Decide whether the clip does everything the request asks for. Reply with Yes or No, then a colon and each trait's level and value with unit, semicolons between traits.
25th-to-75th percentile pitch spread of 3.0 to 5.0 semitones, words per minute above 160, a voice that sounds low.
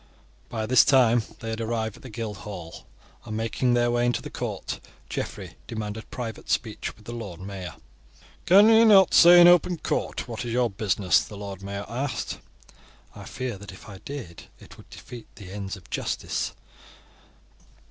Yes: average, 3.7 semitones; average, 175 wpm; low, 115 Hz